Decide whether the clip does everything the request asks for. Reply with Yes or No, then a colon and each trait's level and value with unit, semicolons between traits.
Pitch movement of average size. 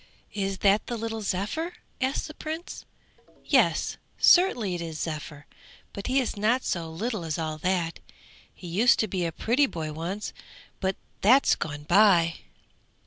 No: wide, 6.0 semitones